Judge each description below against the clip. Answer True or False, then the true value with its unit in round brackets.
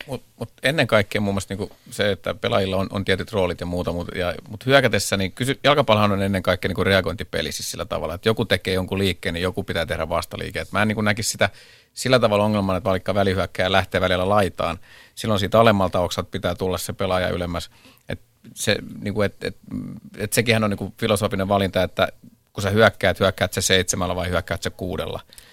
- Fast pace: True (205 wpm)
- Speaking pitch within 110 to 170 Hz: False (95 Hz)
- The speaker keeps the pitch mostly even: True (2.2 semitones)